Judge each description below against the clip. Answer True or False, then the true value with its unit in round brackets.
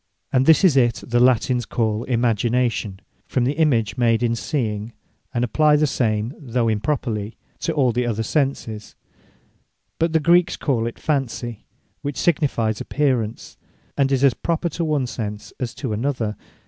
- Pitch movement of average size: True (4.1 semitones)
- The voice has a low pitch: True (125 Hz)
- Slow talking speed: False (160 wpm)